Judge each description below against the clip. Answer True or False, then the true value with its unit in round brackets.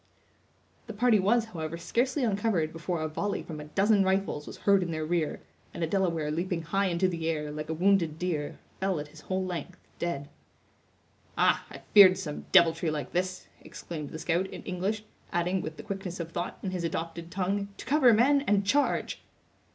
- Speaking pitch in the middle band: True (180 Hz)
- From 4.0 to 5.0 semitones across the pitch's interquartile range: False (3.4 semitones)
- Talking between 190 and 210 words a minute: True (195 wpm)